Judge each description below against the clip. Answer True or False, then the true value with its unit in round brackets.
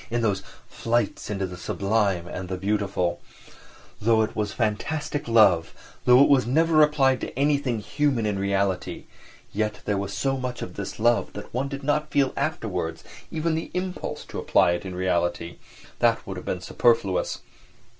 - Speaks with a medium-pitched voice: False (110 Hz)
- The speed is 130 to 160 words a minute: False (170 wpm)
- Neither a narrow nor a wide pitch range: False (5.8 semitones)